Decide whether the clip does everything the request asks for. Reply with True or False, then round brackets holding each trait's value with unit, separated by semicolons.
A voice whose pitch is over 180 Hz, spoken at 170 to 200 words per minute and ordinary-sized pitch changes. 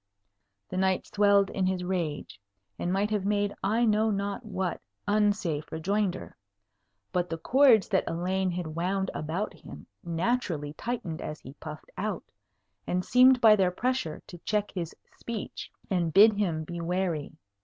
False (190 Hz; 155 wpm; 3.5 semitones)